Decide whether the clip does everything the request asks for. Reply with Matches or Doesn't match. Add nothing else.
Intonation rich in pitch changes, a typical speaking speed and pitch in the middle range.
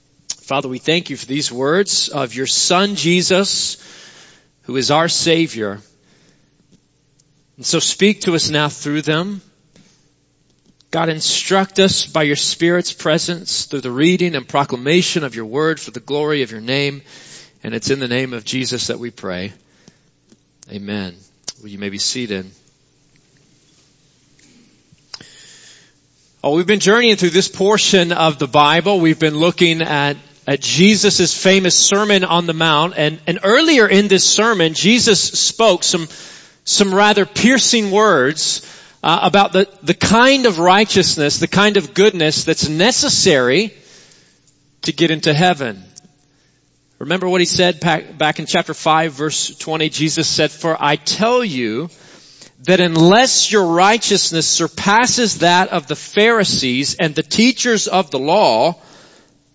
Doesn't match